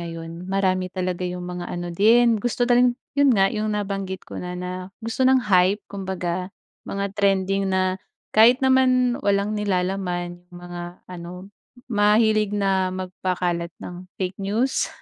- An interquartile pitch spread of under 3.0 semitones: Yes, narrow, 2.5 semitones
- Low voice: No, high, 190 Hz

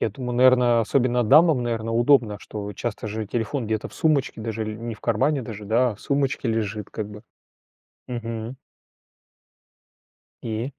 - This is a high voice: No, low, 115 Hz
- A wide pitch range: No, narrow, 2.6 semitones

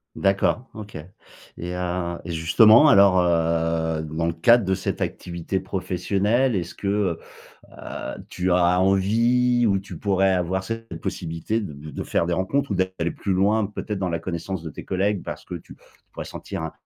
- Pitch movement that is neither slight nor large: Yes, average, 3.2 semitones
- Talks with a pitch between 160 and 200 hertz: No, very low, 95 Hz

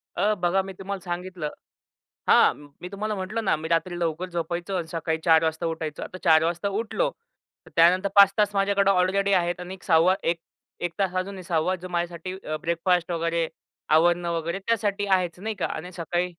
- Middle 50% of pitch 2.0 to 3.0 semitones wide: Yes, narrow, 2.5 semitones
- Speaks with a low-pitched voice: No, medium, 180 Hz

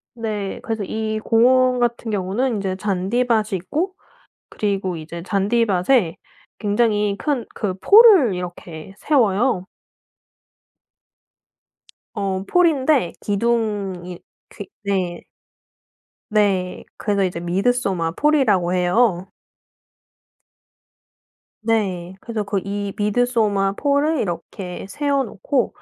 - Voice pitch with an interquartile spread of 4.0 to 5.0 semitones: Yes, average, 4.4 semitones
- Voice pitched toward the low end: No, high, 205 Hz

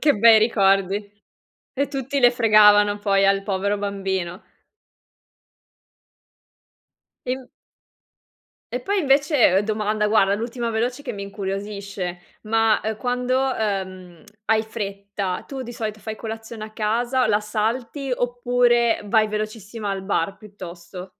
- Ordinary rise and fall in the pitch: Yes, average, 3.3 semitones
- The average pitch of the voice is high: Yes, high, 215 Hz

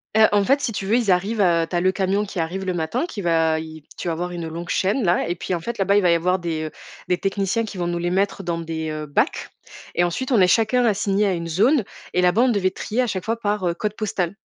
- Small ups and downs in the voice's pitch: No, average, 3.4 semitones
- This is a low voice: No, medium, 185 Hz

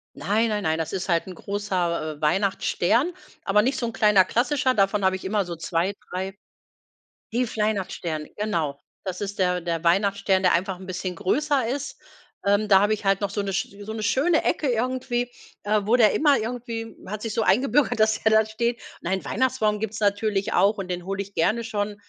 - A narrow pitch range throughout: No, average, 3.2 semitones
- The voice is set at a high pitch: Yes, high, 205 Hz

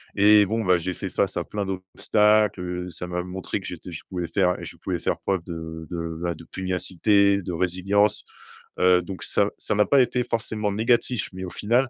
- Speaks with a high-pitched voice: No, very low, 95 Hz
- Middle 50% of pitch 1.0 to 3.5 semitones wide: Yes, average, 2.8 semitones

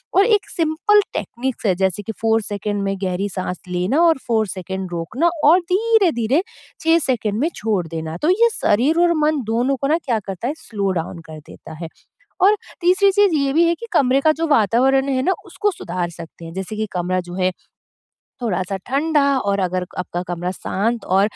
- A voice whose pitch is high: Yes, high, 230 Hz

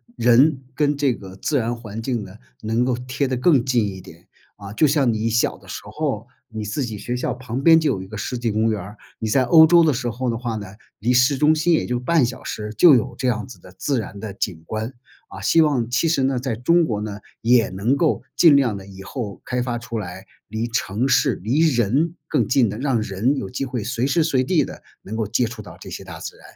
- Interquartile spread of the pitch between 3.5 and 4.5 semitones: Yes, average, 3.9 semitones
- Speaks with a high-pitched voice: No, low, 120 Hz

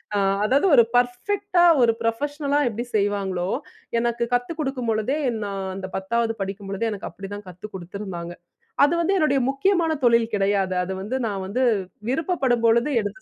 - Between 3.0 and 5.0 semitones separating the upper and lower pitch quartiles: No, wide, 5.6 semitones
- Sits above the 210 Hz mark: Yes, high, 230 Hz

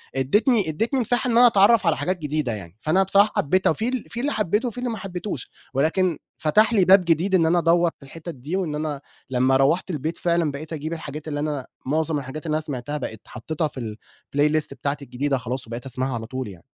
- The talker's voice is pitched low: No, medium, 155 Hz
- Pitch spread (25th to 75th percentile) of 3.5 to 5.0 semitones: No, wide, 5.4 semitones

